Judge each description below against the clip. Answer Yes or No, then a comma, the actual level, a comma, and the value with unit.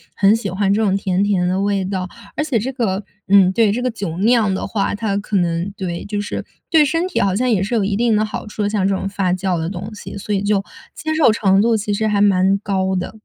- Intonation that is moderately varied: No, narrow, 2.3 semitones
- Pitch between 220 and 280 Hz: No, high, 200 Hz